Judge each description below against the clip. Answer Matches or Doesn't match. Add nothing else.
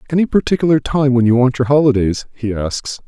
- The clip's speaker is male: Matches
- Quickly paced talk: Doesn't match